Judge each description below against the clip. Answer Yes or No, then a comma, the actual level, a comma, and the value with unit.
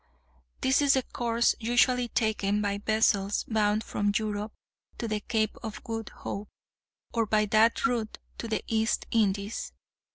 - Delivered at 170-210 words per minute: No, average, 150 wpm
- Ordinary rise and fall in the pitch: No, narrow, 1.9 semitones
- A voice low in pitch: No, high, 220 Hz